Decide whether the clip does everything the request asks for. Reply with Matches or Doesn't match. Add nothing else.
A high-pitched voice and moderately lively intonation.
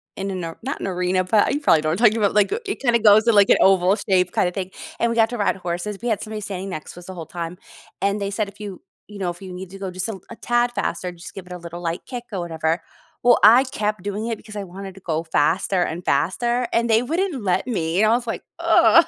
Matches